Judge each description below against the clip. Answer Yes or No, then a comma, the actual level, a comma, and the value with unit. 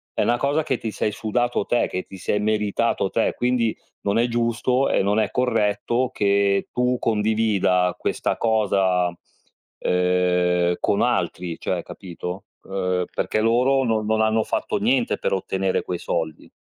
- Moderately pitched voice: No, low, 105 Hz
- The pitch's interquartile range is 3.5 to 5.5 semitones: Yes, average, 4.4 semitones